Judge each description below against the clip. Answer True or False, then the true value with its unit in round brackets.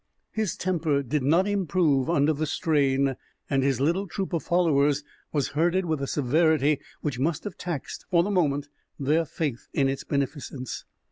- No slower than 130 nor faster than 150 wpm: False (165 wpm)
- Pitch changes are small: False (3.6 semitones)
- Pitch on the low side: False (150 Hz)